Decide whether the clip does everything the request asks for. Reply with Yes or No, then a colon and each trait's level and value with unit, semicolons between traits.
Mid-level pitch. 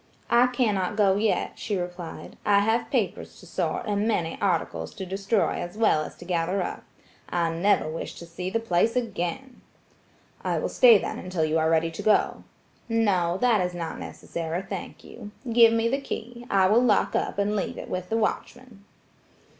No: high, 200 Hz